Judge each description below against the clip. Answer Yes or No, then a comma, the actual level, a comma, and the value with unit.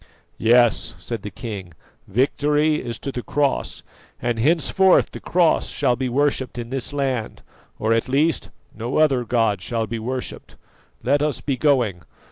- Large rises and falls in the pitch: No, average, 3.9 semitones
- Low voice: Yes, low, 125 Hz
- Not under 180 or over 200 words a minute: No, average, 155 wpm